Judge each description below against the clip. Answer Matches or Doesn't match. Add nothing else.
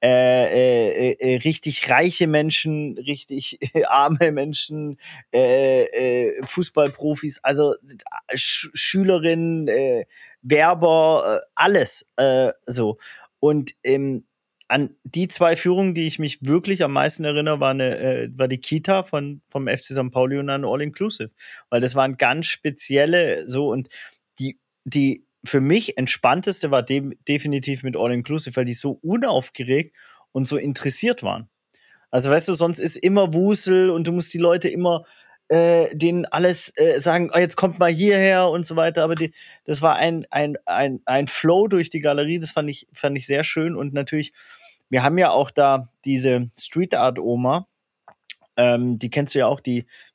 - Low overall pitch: Doesn't match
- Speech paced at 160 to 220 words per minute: Matches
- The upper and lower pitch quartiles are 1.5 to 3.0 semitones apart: Doesn't match